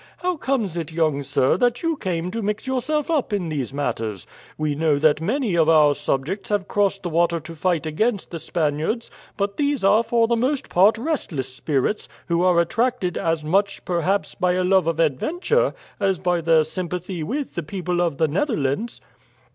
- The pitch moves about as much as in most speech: No, wide, 5.9 semitones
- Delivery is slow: No, average, 185 wpm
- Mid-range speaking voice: Yes, medium, 180 Hz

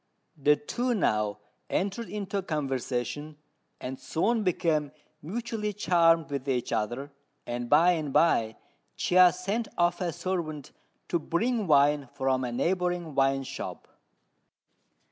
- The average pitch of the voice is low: No, medium, 165 Hz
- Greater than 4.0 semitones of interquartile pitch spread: Yes, average, 5.3 semitones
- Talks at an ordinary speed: No, slow, 125 wpm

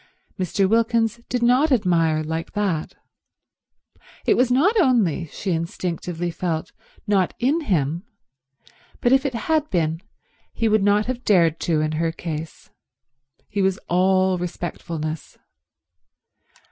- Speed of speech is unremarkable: No, slow, 125 wpm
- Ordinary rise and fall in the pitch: No, wide, 5.9 semitones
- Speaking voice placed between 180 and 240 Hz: Yes, medium, 185 Hz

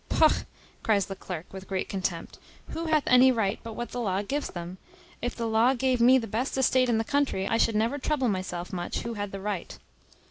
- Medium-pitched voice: No, high, 225 Hz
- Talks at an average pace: No, fast, 220 wpm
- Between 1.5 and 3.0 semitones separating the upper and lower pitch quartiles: No, average, 4.7 semitones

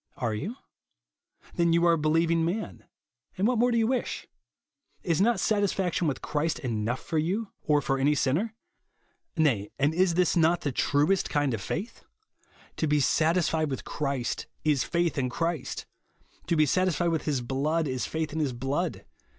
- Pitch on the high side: No, medium, 160 Hz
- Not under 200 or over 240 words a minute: No, average, 175 wpm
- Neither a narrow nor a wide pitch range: Yes, average, 3.7 semitones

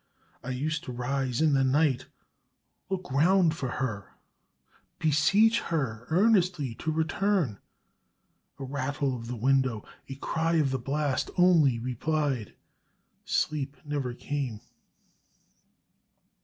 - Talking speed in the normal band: No, slow, 115 wpm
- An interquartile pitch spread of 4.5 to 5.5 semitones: No, average, 3.9 semitones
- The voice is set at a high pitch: No, medium, 140 Hz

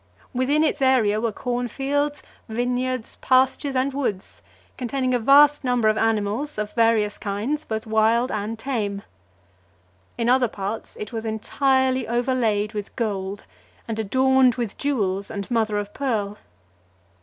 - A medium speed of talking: Yes, average, 145 wpm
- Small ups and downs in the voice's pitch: No, average, 3.7 semitones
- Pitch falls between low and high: No, high, 235 Hz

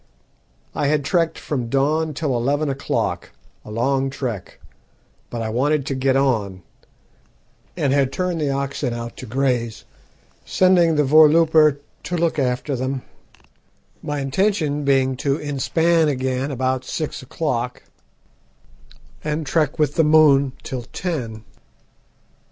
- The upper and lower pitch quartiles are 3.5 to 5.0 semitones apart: No, average, 3.0 semitones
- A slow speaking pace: Yes, slow, 130 wpm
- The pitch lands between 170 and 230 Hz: No, medium, 140 Hz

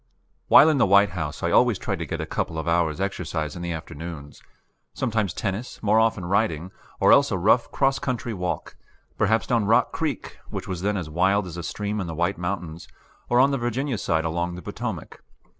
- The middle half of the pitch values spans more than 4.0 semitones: Yes, average, 4.7 semitones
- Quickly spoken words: Yes, fast, 210 wpm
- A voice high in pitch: No, very low, 95 Hz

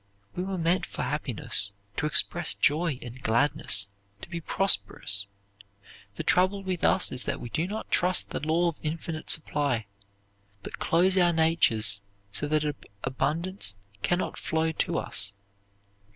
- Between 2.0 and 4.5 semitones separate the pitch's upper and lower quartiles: No, average, 5.3 semitones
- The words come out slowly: No, average, 145 wpm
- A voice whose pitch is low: No, medium, 160 Hz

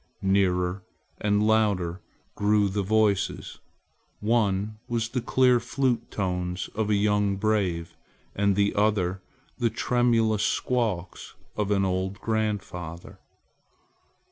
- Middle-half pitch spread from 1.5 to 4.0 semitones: Yes, average, 2.7 semitones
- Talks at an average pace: No, slow, 110 wpm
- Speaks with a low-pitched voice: Yes, low, 105 Hz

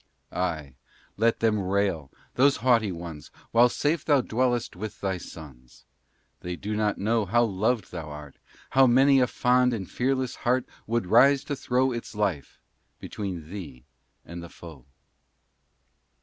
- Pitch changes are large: Yes, wide, 6.1 semitones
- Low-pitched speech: Yes, low, 105 Hz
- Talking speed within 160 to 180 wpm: No, average, 150 wpm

